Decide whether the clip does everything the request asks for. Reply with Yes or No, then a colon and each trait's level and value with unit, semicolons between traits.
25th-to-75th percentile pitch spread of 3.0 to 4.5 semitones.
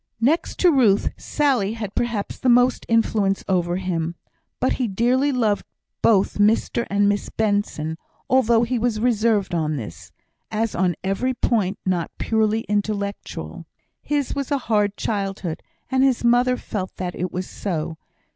Yes: average, 4.2 semitones